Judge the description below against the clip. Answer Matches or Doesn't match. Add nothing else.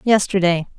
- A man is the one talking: Doesn't match